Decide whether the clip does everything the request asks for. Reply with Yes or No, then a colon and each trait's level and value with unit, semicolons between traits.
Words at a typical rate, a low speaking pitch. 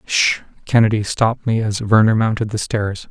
Yes: average, 175 wpm; low, 110 Hz